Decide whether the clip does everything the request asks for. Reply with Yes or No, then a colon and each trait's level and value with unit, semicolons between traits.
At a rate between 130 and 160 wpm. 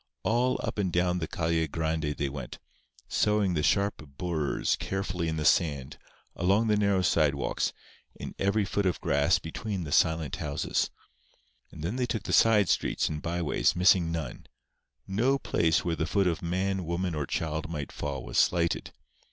No: average, 175 wpm